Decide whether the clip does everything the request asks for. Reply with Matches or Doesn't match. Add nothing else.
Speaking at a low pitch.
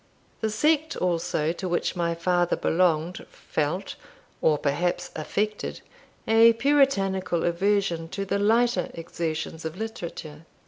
Doesn't match